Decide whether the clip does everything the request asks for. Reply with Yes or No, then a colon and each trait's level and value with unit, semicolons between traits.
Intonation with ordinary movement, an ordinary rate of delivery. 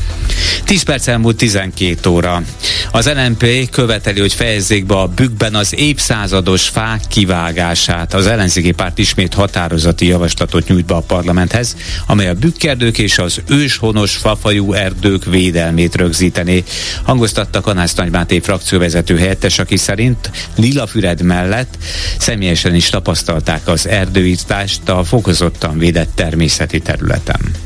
Yes: average, 3.9 semitones; average, 120 wpm